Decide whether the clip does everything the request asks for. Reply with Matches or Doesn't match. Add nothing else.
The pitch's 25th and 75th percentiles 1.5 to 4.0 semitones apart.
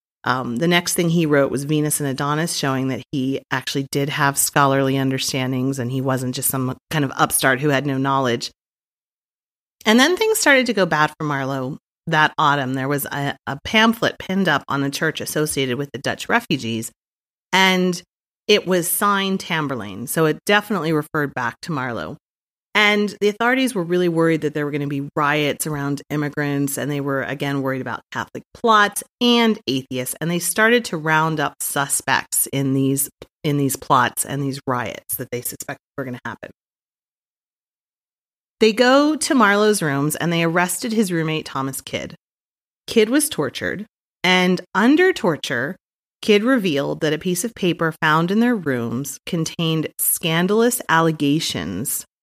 Doesn't match